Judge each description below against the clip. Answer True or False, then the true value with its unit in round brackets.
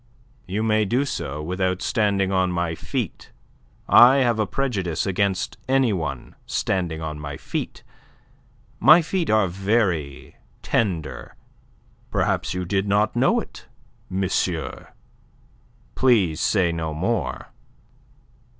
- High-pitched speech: False (95 Hz)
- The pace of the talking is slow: True (115 wpm)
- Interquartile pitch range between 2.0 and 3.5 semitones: False (4.2 semitones)